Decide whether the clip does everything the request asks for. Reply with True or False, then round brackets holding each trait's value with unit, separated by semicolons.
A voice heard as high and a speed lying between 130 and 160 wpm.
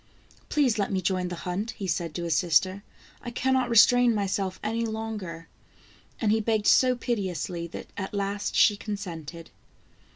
False (200 Hz; 175 wpm)